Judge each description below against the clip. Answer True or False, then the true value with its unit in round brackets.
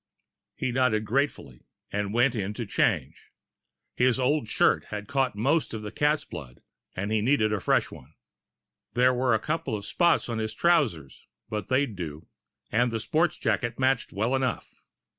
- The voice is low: True (115 Hz)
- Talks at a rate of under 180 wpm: True (170 wpm)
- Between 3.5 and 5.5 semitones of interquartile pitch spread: True (4.1 semitones)